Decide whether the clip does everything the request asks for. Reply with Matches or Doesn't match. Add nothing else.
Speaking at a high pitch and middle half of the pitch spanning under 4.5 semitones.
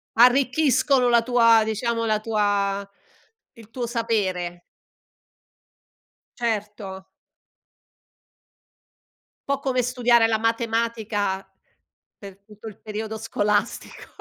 Matches